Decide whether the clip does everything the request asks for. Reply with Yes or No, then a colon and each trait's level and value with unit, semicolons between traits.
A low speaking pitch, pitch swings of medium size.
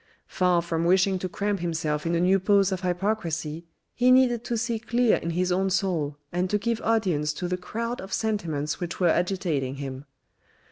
No: medium, 180 Hz; average, 3.8 semitones